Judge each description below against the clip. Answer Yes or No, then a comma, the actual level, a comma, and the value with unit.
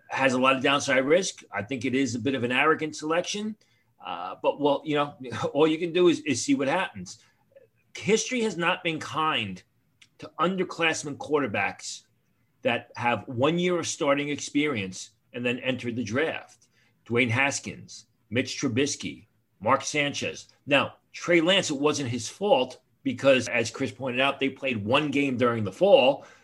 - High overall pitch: No, medium, 140 Hz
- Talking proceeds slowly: No, average, 170 wpm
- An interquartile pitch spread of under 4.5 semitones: No, wide, 5.4 semitones